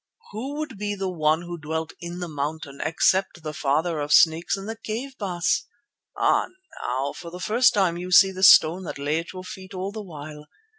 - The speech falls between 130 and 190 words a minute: No, fast, 205 wpm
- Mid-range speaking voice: Yes, medium, 175 Hz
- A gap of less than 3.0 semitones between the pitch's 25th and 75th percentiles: No, average, 3.8 semitones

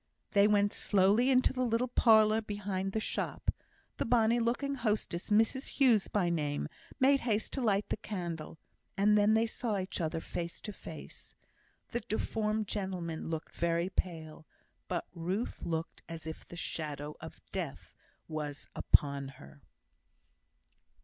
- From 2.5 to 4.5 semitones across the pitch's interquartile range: No, average, 5.0 semitones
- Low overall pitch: No, high, 205 Hz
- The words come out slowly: No, average, 145 wpm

